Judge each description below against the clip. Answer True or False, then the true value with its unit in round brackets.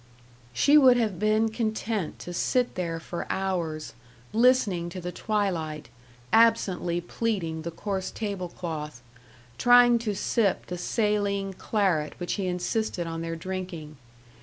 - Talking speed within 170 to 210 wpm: False (135 wpm)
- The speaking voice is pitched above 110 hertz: True (190 Hz)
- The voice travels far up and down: False (4.4 semitones)